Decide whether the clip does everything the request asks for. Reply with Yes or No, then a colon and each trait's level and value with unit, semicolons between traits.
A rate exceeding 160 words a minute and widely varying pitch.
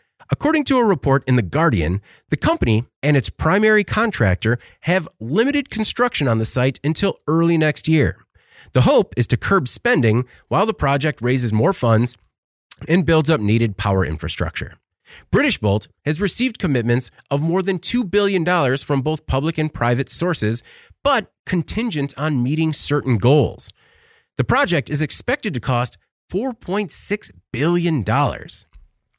No: average, 145 wpm; wide, 7.2 semitones